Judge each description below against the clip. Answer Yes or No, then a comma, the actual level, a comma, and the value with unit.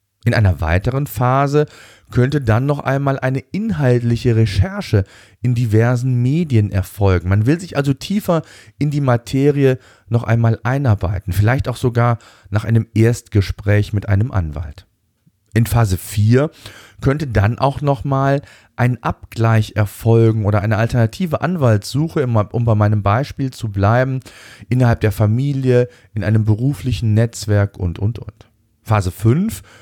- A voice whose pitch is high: No, low, 115 Hz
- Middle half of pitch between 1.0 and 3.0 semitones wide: No, average, 3.8 semitones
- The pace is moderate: Yes, average, 135 wpm